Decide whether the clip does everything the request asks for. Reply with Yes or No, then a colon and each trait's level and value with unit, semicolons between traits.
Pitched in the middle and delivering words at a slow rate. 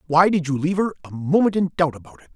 No: medium, 160 Hz; fast, 280 wpm